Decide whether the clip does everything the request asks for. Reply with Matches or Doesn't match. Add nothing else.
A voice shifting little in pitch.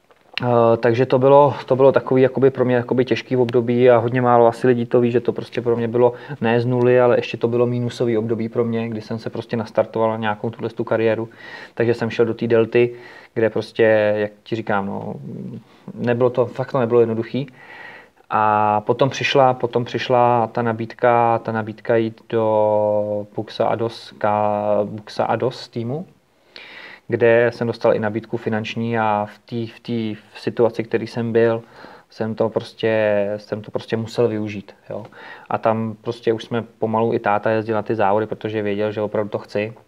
Matches